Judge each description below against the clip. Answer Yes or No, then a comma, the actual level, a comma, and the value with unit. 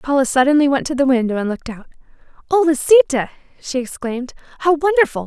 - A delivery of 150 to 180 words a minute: Yes, average, 170 wpm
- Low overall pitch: No, very high, 280 Hz